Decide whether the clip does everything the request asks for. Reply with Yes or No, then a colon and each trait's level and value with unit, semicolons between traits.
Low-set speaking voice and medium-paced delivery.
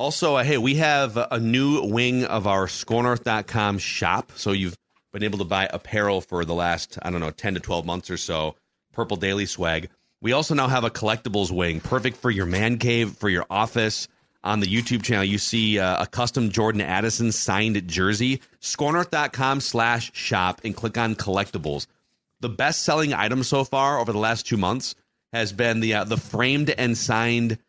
Yes: low, 110 Hz; average, 190 wpm